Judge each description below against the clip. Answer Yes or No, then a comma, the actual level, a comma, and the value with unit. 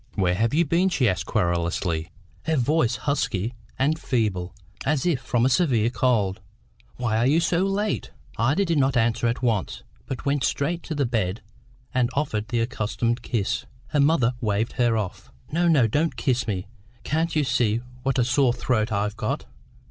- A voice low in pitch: Yes, low, 120 Hz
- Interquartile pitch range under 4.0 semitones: No, average, 5.1 semitones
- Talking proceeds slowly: No, average, 180 wpm